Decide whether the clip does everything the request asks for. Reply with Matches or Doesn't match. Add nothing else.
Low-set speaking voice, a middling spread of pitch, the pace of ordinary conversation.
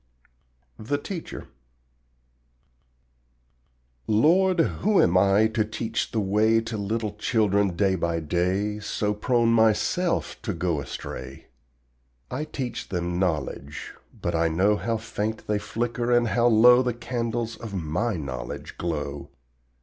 Doesn't match